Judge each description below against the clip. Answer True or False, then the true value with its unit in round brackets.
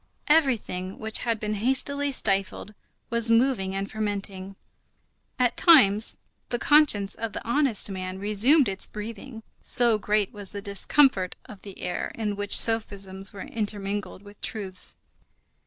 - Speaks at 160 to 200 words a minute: False (140 wpm)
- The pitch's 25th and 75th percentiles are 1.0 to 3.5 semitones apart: True (2.9 semitones)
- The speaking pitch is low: False (210 Hz)